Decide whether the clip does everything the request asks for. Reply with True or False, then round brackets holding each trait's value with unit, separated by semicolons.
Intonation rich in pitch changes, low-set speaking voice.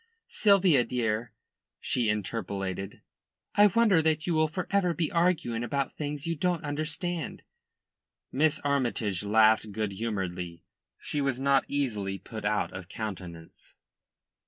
True (7.1 semitones; 125 Hz)